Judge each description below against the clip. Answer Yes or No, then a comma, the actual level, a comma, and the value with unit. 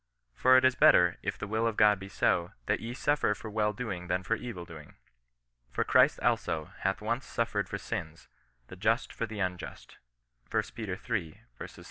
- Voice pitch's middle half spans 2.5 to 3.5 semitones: No, average, 4.3 semitones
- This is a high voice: No, low, 105 Hz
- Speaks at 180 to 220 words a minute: Yes, average, 185 wpm